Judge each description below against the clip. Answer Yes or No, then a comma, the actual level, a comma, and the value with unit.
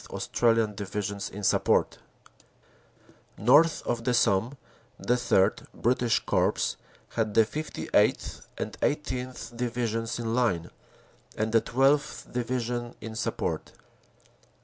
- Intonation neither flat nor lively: No, narrow, 2.2 semitones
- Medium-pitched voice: No, low, 115 Hz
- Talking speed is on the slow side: Yes, slow, 110 wpm